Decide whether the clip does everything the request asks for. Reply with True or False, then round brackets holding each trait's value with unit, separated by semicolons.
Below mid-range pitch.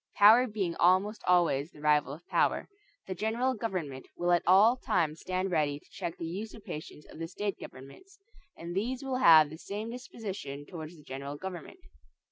False (180 Hz)